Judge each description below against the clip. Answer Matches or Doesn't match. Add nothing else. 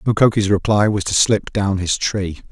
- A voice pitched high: Doesn't match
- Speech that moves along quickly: Doesn't match